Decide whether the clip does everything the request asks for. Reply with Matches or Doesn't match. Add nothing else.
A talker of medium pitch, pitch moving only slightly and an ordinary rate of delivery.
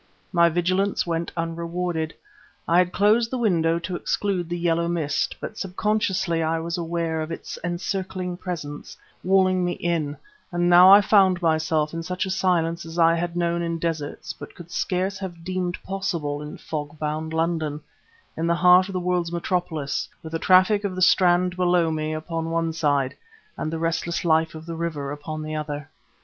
Matches